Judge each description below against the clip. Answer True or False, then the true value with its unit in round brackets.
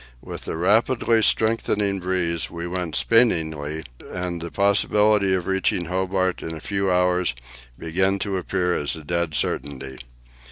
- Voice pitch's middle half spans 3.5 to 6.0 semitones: False (2.8 semitones)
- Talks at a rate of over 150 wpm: False (145 wpm)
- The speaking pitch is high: False (90 Hz)